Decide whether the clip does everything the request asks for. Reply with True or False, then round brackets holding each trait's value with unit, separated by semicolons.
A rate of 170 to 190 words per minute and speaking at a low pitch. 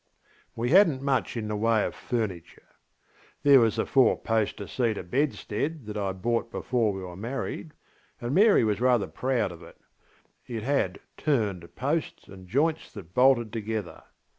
False (160 wpm; 115 Hz)